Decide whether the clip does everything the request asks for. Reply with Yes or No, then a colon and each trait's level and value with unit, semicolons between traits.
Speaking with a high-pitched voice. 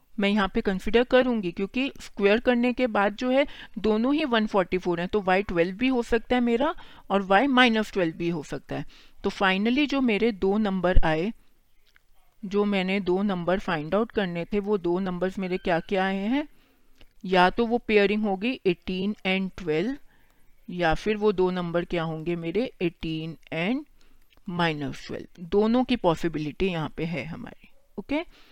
Yes: high, 200 Hz